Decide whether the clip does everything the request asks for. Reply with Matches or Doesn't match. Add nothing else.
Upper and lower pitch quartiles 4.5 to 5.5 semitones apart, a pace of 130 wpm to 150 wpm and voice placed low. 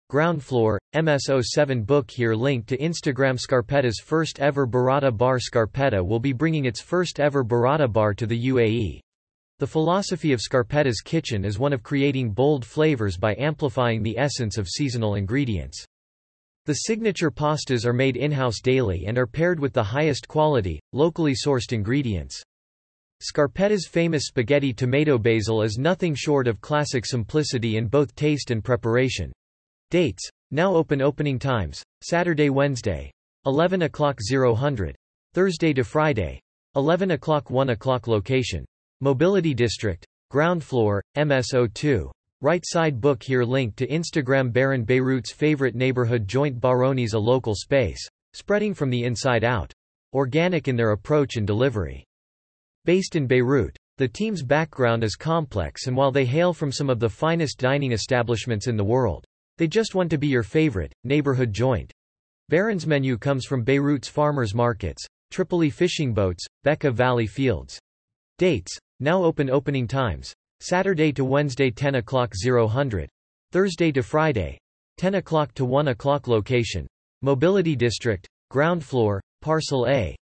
Matches